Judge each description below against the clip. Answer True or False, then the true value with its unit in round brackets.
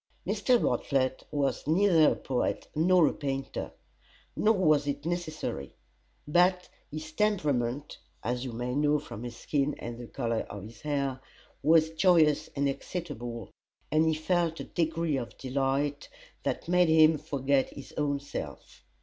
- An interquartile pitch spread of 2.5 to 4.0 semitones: True (3.4 semitones)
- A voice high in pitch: False (145 Hz)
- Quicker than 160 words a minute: False (150 wpm)